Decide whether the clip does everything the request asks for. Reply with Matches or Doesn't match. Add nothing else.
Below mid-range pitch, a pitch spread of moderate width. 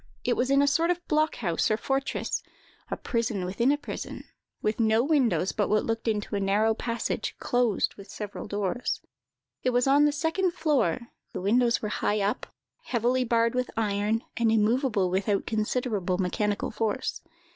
Doesn't match